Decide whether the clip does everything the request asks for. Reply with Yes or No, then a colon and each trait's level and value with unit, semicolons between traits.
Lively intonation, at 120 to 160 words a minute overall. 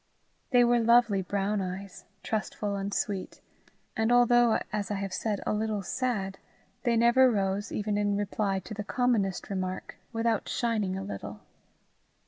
No: average, 3.0 semitones; average, 150 wpm